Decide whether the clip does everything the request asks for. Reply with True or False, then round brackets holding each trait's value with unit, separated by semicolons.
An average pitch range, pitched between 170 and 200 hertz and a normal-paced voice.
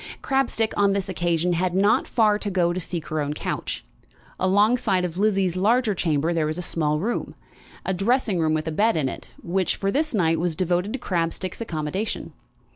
True (3.9 semitones; 185 Hz; 195 wpm)